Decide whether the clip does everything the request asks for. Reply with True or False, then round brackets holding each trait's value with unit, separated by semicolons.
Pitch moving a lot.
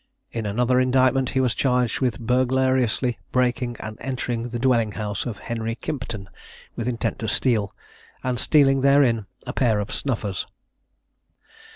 False (2.4 semitones)